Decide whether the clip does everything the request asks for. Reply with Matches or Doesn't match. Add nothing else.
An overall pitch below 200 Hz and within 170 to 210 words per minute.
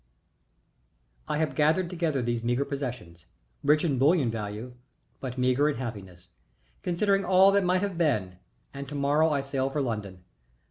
Doesn't match